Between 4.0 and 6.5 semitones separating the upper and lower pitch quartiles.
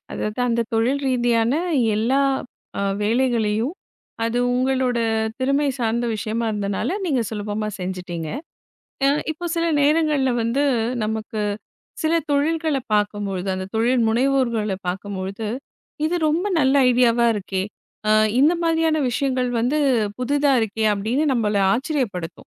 Yes: average, 4.6 semitones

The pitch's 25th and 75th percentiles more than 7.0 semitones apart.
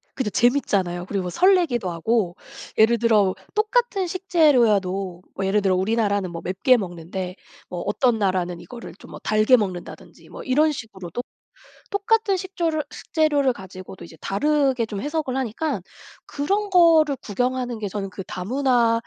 Yes: wide, 7.6 semitones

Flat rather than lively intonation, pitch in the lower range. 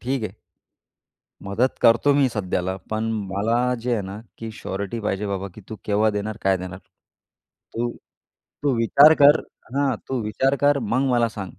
No: average, 3.8 semitones; low, 110 Hz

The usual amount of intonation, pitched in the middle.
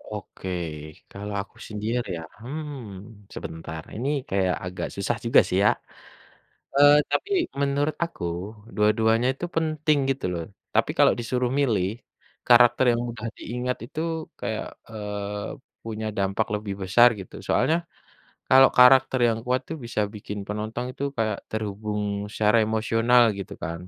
No: average, 3.4 semitones; low, 110 Hz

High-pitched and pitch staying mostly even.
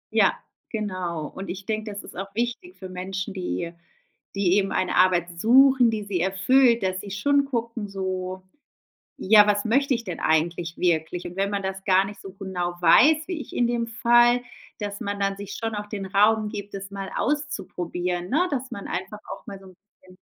No: high, 200 Hz; average, 3.8 semitones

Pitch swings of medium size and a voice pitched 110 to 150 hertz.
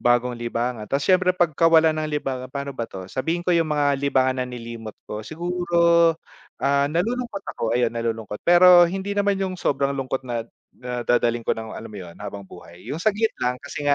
No: wide, 6.4 semitones; medium, 140 Hz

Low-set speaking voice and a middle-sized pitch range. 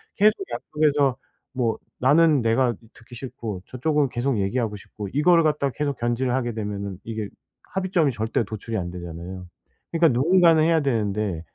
No: low, 120 Hz; wide, 5.9 semitones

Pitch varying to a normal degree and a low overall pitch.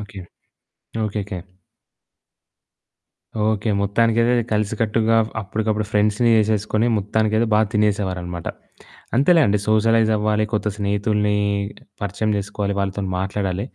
No: narrow, 1.5 semitones; low, 105 Hz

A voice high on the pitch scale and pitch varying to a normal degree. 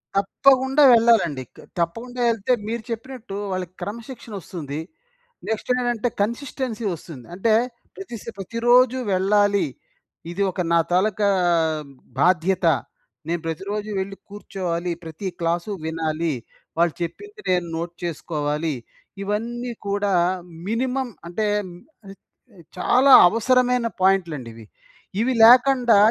No: high, 205 Hz; wide, 5.8 semitones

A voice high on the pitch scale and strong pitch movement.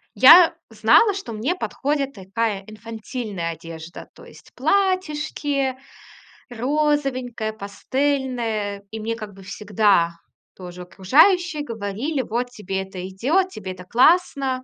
Yes: high, 230 Hz; wide, 6.3 semitones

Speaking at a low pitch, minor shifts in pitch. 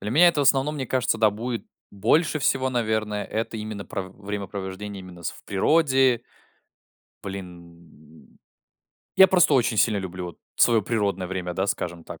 No: low, 105 Hz; average, 5.0 semitones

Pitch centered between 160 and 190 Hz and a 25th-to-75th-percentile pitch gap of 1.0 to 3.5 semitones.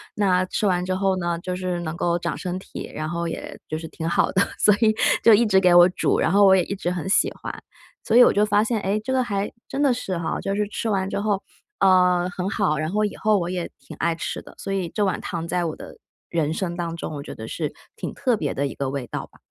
Yes: medium, 185 Hz; average, 3.1 semitones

